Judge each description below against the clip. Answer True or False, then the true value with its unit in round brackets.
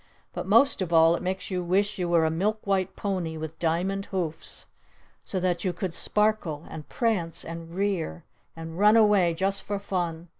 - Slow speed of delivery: False (185 wpm)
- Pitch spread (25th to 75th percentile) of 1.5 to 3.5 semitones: True (3.2 semitones)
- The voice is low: False (180 Hz)